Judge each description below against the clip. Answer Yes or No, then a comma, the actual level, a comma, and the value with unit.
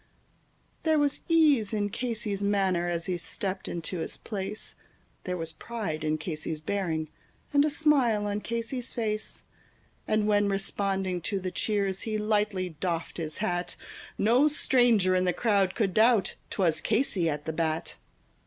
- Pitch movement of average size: Yes, average, 4.0 semitones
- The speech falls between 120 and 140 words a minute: No, average, 155 wpm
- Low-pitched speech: No, high, 200 Hz